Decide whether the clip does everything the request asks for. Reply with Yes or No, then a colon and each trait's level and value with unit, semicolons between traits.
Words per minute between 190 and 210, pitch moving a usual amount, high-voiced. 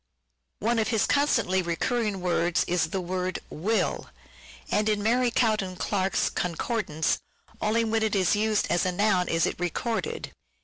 No: average, 160 wpm; average, 3.7 semitones; high, 205 Hz